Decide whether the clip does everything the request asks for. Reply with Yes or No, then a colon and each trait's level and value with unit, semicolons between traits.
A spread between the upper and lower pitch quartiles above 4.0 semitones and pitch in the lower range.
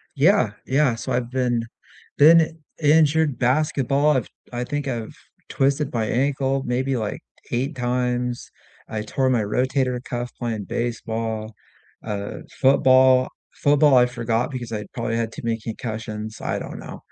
No: average, 2.9 semitones; low, 125 Hz